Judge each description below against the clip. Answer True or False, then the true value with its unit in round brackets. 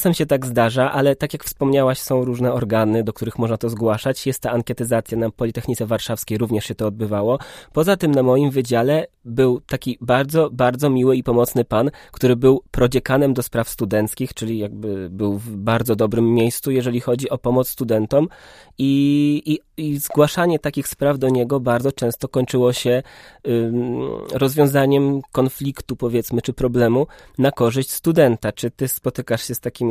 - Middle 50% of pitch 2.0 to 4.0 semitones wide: True (2.9 semitones)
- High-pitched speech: False (125 Hz)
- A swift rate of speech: True (170 wpm)